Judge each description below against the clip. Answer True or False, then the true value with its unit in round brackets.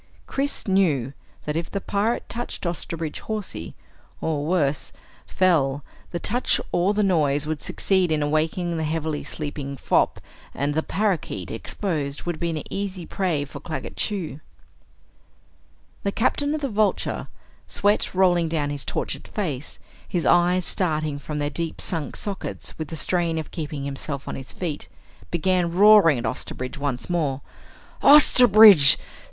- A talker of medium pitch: True (165 Hz)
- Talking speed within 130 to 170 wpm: True (145 wpm)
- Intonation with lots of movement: False (4.5 semitones)